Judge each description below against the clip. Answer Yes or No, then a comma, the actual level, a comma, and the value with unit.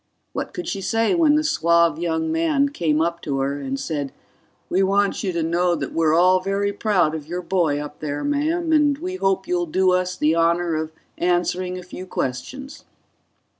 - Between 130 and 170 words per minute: No, average, 195 wpm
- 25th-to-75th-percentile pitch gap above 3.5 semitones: Yes, average, 4.0 semitones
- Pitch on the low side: No, medium, 180 Hz